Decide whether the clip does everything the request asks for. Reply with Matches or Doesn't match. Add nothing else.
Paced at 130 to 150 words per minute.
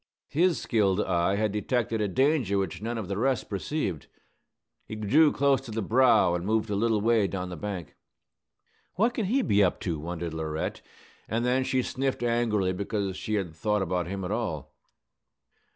Doesn't match